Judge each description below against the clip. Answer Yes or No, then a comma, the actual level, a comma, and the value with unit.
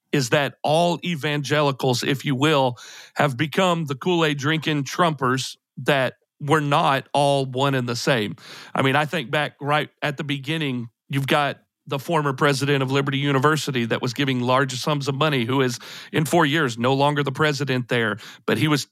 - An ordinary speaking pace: Yes, average, 185 wpm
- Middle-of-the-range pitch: Yes, medium, 145 Hz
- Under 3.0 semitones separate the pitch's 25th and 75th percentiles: Yes, narrow, 2.4 semitones